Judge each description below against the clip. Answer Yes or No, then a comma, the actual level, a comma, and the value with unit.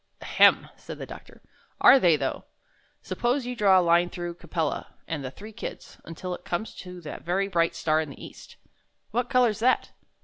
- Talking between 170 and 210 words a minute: Yes, average, 190 wpm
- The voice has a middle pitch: Yes, medium, 180 Hz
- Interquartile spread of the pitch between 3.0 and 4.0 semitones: No, average, 4.8 semitones